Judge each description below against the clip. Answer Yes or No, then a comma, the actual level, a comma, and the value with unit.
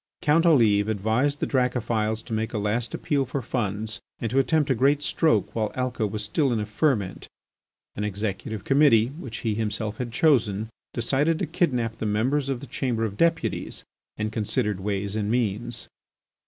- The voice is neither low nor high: No, low, 115 Hz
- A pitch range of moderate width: Yes, average, 4.1 semitones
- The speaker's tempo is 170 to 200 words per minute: Yes, average, 175 wpm